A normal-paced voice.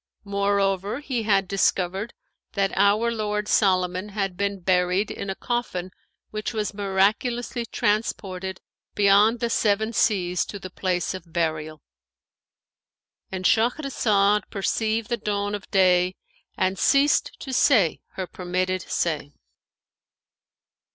No: slow, 115 wpm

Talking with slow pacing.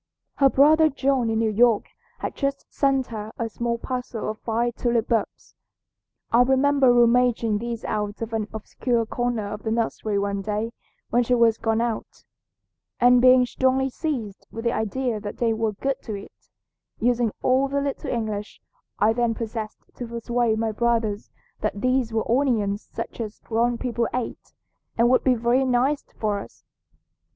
No: average, 170 wpm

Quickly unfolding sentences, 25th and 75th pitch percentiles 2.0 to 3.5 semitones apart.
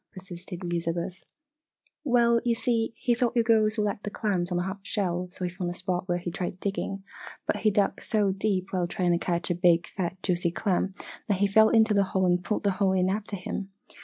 Yes: fast, 220 wpm; average, 2.9 semitones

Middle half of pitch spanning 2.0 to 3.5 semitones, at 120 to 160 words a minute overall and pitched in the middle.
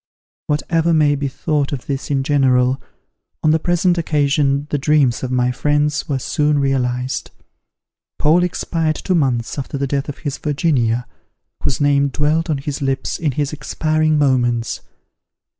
Yes: narrow, 2.4 semitones; average, 155 wpm; medium, 145 Hz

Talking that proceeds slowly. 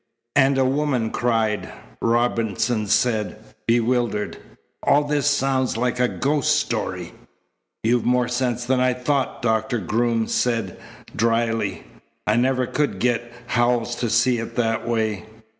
Yes: slow, 130 wpm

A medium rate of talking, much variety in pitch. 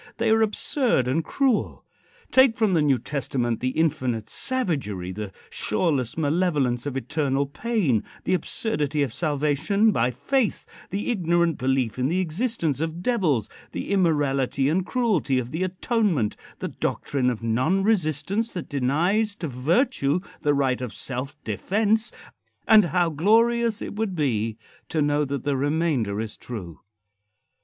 Yes: average, 145 wpm; wide, 7.2 semitones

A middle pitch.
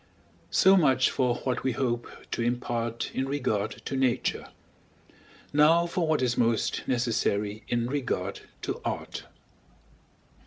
No: low, 125 Hz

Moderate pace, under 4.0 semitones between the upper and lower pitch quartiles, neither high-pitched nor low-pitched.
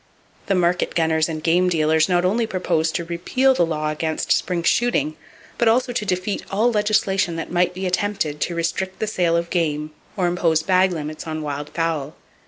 Yes: average, 190 wpm; average, 3.1 semitones; medium, 175 Hz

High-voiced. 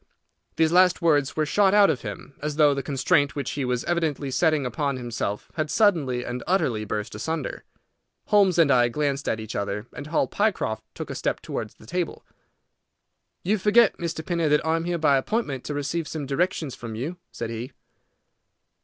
No: medium, 150 Hz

